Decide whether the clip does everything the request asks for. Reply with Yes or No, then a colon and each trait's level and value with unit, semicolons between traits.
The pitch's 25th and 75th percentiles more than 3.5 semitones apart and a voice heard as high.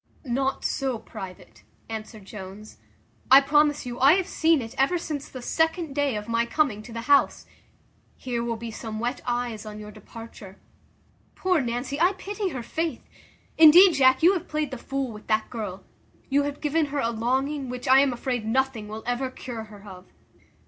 Yes: average, 4.4 semitones; very high, 255 Hz